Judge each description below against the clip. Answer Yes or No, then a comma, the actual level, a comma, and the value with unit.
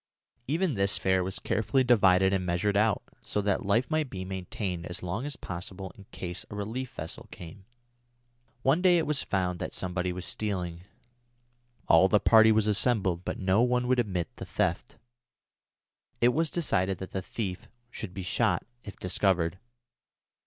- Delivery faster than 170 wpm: No, average, 165 wpm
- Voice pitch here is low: Yes, low, 100 Hz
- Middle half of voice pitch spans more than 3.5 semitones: Yes, average, 4.4 semitones